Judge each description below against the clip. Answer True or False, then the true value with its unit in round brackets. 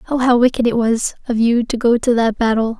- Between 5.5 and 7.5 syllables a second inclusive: True (5.7 syllables/s)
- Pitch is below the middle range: False (235 Hz)